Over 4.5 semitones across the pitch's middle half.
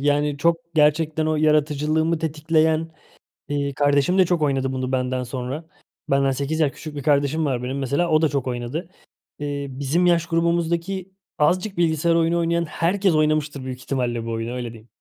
No: average, 3.3 semitones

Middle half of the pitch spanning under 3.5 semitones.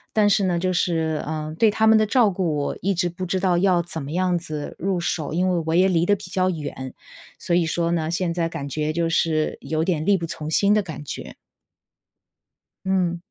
Yes: average, 2.8 semitones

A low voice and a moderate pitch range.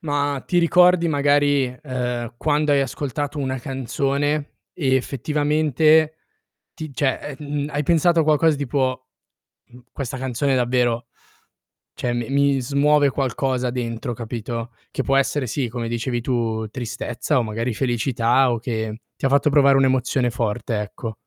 Yes: low, 130 Hz; average, 3.2 semitones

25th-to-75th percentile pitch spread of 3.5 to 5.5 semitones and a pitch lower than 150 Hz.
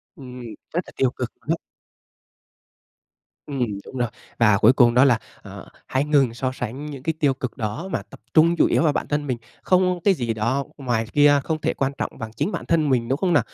Yes: average, 3.8 semitones; low, 135 Hz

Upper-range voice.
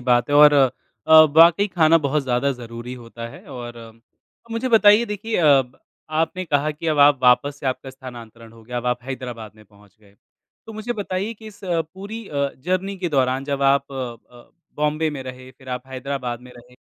No: low, 135 Hz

